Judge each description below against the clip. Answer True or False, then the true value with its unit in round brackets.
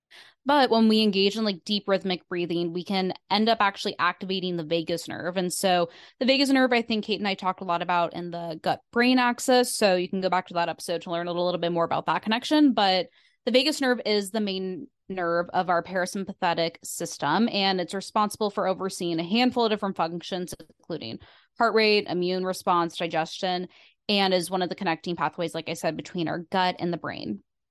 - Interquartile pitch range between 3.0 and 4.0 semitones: True (3.5 semitones)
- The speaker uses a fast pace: True (210 wpm)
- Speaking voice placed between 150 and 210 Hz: True (185 Hz)